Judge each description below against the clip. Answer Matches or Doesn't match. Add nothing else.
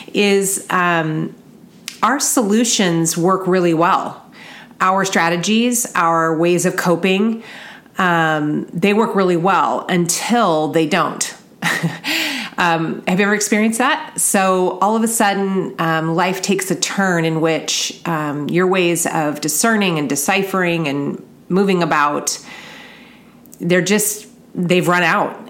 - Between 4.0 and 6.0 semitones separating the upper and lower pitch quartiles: Matches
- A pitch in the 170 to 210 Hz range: Matches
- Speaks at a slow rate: Matches